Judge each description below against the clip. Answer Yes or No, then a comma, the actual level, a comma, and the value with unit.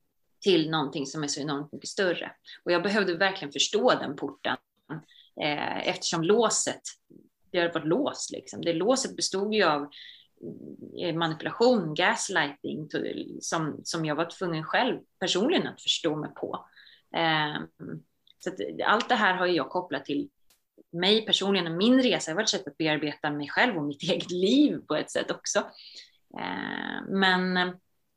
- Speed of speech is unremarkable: Yes, average, 160 wpm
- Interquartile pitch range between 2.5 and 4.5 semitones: Yes, average, 4.1 semitones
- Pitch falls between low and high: Yes, medium, 175 Hz